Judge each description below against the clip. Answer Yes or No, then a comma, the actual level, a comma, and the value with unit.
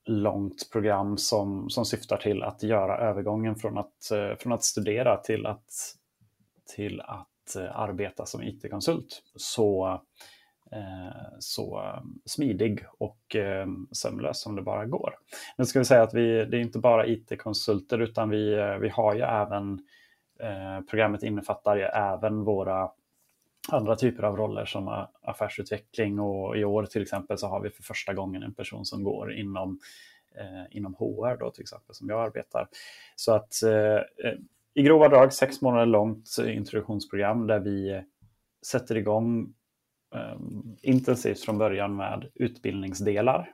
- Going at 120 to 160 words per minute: Yes, average, 150 wpm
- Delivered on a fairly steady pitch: Yes, narrow, 2.2 semitones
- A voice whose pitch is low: Yes, low, 105 Hz